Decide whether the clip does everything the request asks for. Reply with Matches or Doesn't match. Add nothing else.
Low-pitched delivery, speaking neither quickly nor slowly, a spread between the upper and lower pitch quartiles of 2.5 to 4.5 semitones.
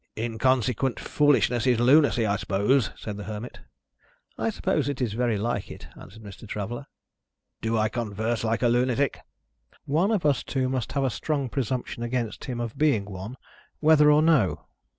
Matches